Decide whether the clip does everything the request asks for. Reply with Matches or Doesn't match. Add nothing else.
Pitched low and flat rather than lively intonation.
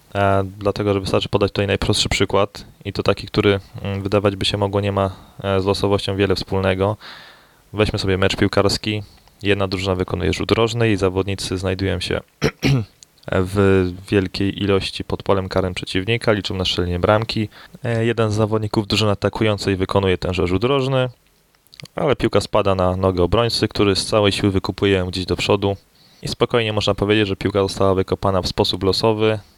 Matches